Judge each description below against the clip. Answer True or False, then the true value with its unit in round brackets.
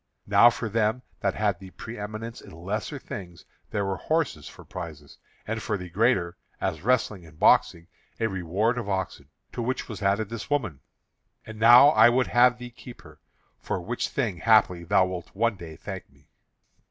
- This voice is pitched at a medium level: False (105 Hz)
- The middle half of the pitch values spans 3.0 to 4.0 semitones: False (4.5 semitones)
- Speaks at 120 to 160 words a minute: False (180 wpm)